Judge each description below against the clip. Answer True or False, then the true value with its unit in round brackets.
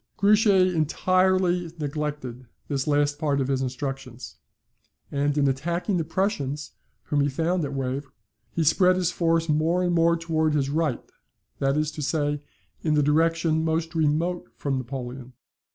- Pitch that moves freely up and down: False (3.2 semitones)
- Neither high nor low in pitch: True (150 Hz)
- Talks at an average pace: True (150 wpm)